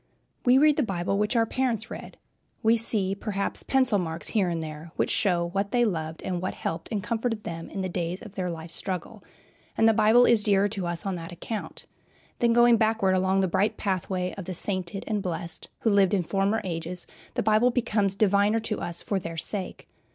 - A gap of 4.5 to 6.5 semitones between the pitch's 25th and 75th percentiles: No, average, 3.8 semitones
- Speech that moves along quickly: Yes, fast, 210 wpm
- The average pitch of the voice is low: No, high, 195 Hz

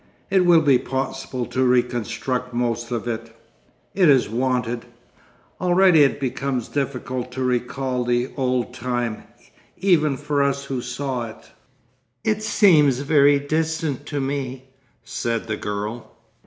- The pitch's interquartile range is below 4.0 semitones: Yes, average, 2.8 semitones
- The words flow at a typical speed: No, slow, 130 wpm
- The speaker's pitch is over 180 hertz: No, low, 130 Hz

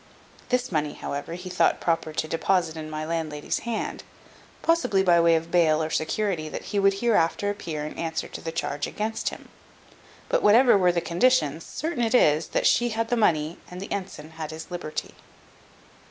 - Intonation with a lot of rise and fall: No, average, 4.8 semitones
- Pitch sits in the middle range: Yes, medium, 170 Hz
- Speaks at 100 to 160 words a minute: No, average, 185 wpm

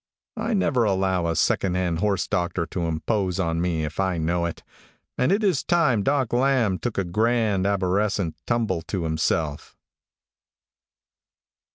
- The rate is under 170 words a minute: Yes, average, 145 wpm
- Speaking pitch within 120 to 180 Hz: No, very low, 95 Hz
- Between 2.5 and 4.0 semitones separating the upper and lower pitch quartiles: No, wide, 5.6 semitones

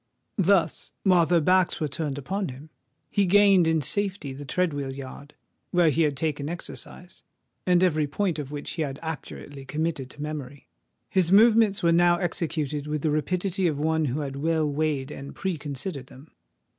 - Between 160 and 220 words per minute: Yes, average, 180 wpm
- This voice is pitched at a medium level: Yes, medium, 155 Hz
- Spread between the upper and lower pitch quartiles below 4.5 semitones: Yes, average, 3.8 semitones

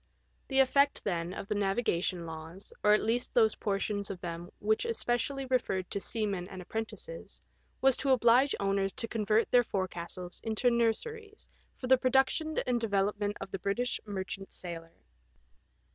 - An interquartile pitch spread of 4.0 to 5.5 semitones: Yes, average, 4.4 semitones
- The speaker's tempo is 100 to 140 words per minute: No, average, 160 wpm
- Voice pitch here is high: Yes, high, 210 Hz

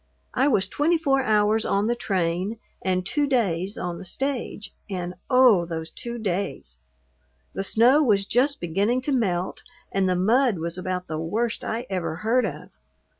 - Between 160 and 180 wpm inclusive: Yes, average, 170 wpm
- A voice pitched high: Yes, high, 205 Hz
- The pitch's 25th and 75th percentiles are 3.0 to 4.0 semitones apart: No, average, 5.3 semitones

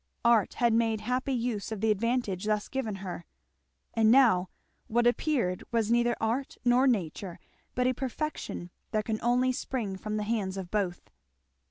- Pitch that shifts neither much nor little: Yes, average, 3.3 semitones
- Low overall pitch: No, high, 225 Hz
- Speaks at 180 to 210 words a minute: No, average, 165 wpm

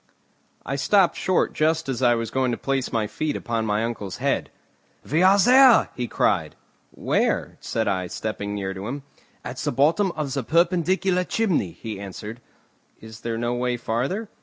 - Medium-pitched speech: No, low, 125 Hz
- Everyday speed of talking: Yes, average, 175 wpm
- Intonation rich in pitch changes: Yes, wide, 7.3 semitones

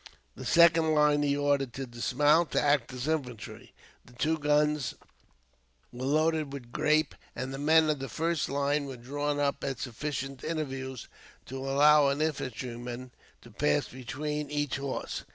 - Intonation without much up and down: Yes, narrow, 2.3 semitones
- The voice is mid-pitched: Yes, medium, 145 Hz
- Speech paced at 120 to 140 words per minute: No, average, 155 wpm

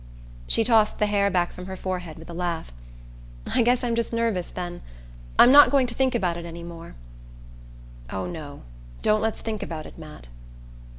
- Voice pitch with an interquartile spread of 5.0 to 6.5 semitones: Yes, average, 5.3 semitones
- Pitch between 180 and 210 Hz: Yes, medium, 185 Hz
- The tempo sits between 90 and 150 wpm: No, average, 185 wpm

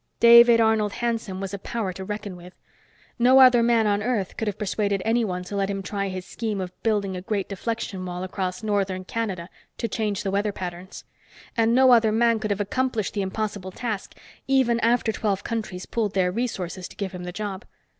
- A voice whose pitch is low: No, high, 205 Hz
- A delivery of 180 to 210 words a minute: Yes, average, 200 wpm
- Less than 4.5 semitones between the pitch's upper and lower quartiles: Yes, average, 3.3 semitones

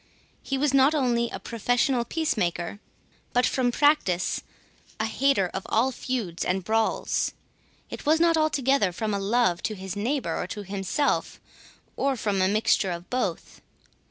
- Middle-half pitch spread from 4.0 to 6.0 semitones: Yes, wide, 5.6 semitones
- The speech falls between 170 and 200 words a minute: No, average, 155 wpm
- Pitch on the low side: No, high, 235 Hz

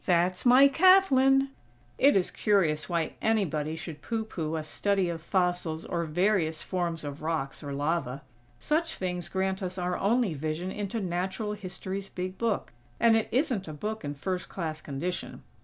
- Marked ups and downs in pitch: No, average, 4.8 semitones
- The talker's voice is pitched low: No, medium, 180 Hz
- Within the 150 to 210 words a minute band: Yes, average, 165 wpm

